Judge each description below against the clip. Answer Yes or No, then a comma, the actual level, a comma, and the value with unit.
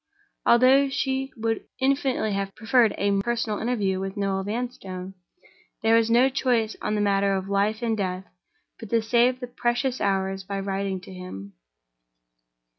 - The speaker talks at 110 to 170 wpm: Yes, average, 155 wpm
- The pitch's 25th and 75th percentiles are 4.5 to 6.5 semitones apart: No, average, 3.8 semitones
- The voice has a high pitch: Yes, high, 215 Hz